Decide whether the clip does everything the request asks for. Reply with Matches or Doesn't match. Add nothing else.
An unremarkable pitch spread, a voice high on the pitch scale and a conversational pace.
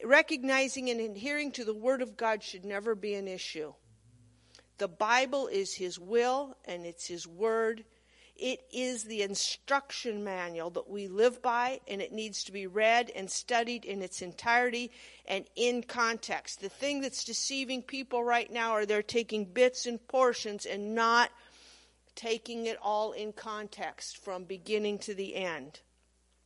Matches